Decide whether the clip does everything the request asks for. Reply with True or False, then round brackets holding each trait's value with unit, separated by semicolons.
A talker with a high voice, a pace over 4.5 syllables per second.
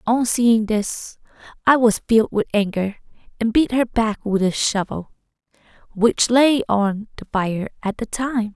False (220 Hz; 4.1 syllables/s)